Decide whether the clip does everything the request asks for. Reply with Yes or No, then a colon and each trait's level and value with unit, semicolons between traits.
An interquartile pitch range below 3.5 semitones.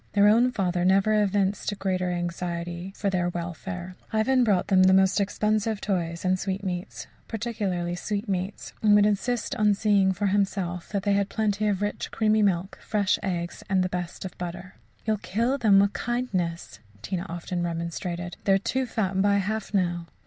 Yes: average, 2.8 semitones